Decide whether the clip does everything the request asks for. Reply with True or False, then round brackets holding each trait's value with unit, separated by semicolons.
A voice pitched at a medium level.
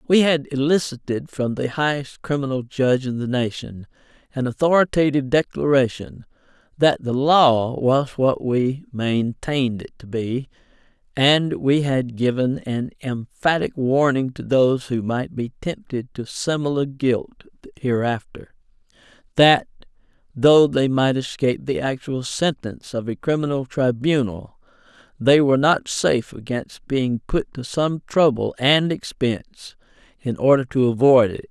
False (130 Hz)